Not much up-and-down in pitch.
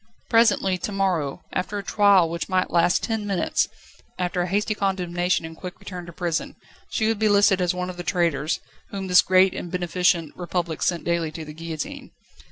Yes: narrow, 2.3 semitones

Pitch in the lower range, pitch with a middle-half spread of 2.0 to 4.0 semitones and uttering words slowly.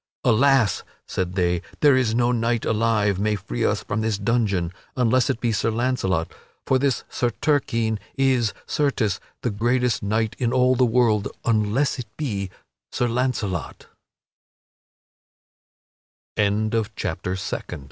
Yes: low, 115 Hz; average, 3.4 semitones; slow, 125 wpm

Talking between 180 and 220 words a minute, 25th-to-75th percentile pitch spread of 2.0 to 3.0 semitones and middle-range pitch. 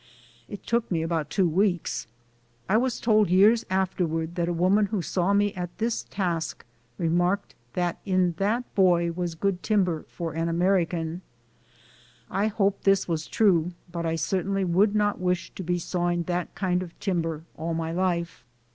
No: average, 165 wpm; average, 2.7 semitones; medium, 180 Hz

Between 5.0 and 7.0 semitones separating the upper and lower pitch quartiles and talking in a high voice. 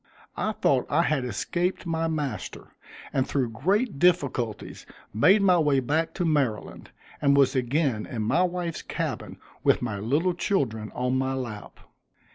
No: wide, 5.6 semitones; medium, 140 Hz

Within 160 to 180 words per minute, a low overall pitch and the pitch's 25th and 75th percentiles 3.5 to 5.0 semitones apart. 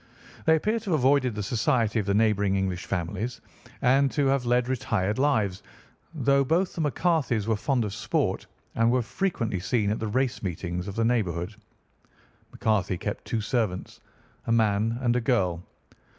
Yes: average, 165 wpm; low, 115 Hz; average, 4.6 semitones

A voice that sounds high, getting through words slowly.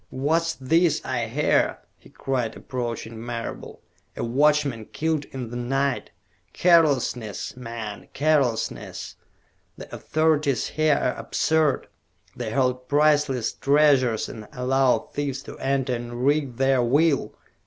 No: low, 135 Hz; slow, 120 wpm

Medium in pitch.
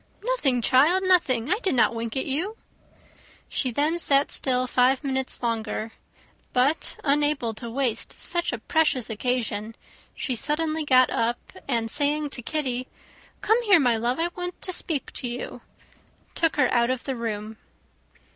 No: very high, 265 Hz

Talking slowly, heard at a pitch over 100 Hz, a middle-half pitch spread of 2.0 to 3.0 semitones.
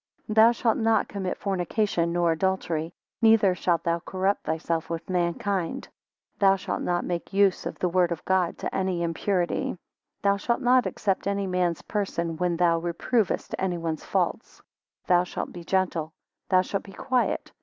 No: average, 170 wpm; medium, 185 Hz; average, 2.7 semitones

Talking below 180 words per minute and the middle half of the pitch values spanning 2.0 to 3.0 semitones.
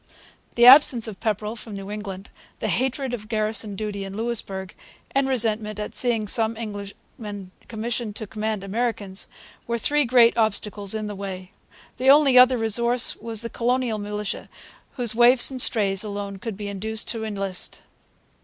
Yes: average, 160 wpm; average, 2.7 semitones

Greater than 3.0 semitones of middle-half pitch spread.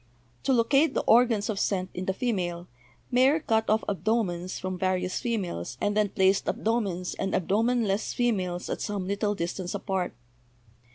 Yes: average, 3.7 semitones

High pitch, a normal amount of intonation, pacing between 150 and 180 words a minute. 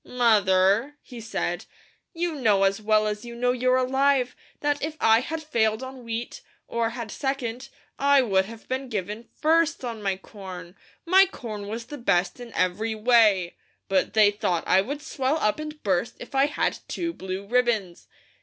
Yes: high, 230 Hz; average, 4.7 semitones; average, 175 wpm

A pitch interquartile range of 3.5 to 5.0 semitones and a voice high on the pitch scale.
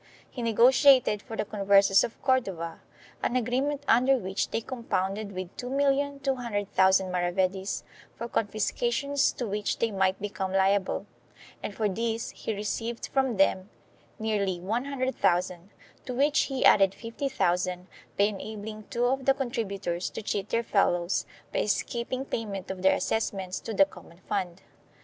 Yes: average, 4.4 semitones; high, 215 Hz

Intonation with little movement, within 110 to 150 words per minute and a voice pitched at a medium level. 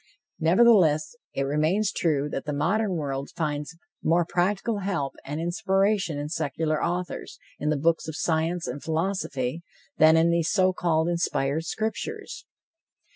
No: average, 3.7 semitones; average, 140 wpm; medium, 165 Hz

